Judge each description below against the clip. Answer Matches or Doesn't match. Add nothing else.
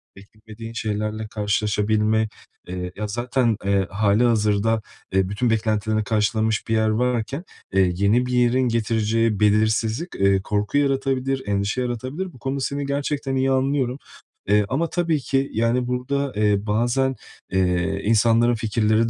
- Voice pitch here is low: Matches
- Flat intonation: Doesn't match